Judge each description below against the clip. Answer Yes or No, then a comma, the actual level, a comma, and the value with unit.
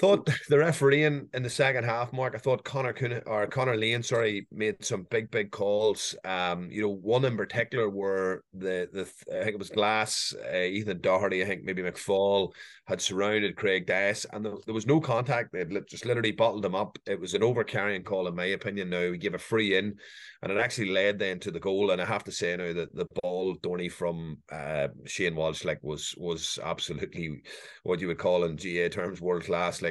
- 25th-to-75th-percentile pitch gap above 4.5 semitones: Yes, average, 5.1 semitones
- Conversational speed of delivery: No, fast, 220 wpm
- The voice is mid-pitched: No, low, 100 Hz